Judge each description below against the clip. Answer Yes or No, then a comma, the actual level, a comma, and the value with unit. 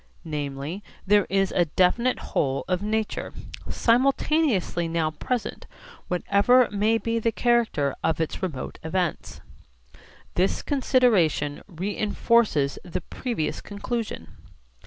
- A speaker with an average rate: No, slow, 105 wpm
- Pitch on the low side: No, high, 195 Hz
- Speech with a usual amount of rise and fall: No, wide, 6.2 semitones